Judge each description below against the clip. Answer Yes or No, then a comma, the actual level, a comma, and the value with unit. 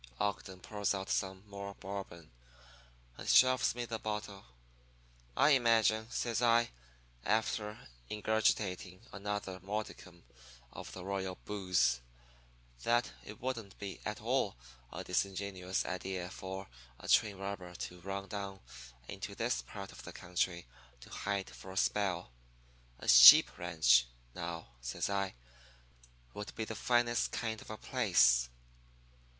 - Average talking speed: No, slow, 130 wpm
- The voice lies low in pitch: Yes, low, 100 Hz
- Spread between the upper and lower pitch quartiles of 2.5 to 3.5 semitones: Yes, average, 2.9 semitones